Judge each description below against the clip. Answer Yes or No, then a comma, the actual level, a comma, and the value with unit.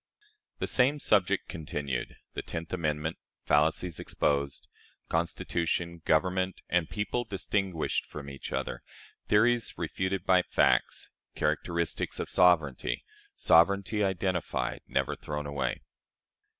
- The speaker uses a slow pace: Yes, slow, 105 wpm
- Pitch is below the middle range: Yes, very low, 85 Hz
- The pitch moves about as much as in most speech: Yes, average, 4.2 semitones